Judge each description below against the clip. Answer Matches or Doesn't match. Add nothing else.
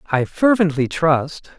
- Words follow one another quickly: Doesn't match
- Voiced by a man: Matches